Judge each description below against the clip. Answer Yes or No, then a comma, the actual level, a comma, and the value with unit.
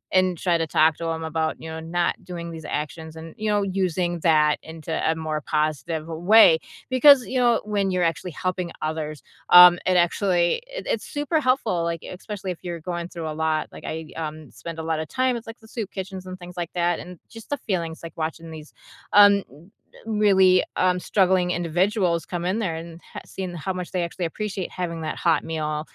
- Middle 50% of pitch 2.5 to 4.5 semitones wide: Yes, average, 2.9 semitones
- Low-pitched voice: No, medium, 175 Hz